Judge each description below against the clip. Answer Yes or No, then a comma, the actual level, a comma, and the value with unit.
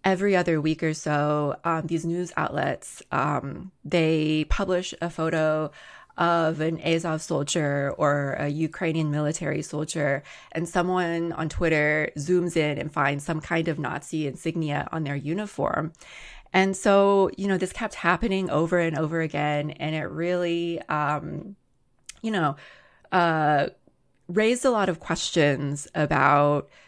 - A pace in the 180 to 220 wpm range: No, average, 140 wpm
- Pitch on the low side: No, medium, 160 Hz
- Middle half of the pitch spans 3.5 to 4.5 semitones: No, average, 2.9 semitones